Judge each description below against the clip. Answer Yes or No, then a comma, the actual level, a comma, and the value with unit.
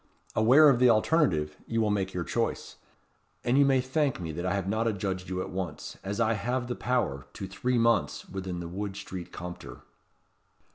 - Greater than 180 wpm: Yes, average, 195 wpm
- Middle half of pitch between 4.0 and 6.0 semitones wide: Yes, average, 4.8 semitones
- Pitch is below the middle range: Yes, low, 105 Hz